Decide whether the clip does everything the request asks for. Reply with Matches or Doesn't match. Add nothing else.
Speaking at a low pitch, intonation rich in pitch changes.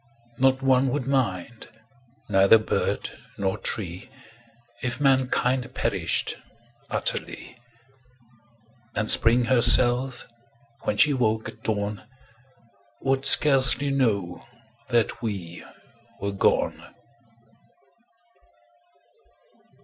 Doesn't match